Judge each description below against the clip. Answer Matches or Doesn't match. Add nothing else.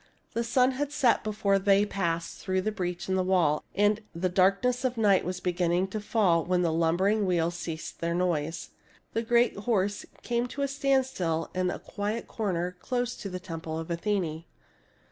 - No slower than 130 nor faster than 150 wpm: Doesn't match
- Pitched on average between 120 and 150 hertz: Doesn't match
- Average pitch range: Matches